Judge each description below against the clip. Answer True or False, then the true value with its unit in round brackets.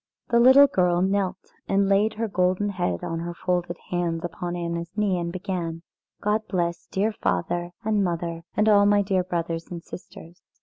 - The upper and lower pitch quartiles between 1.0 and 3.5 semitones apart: True (2.9 semitones)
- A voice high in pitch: False (180 Hz)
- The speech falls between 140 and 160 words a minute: False (175 wpm)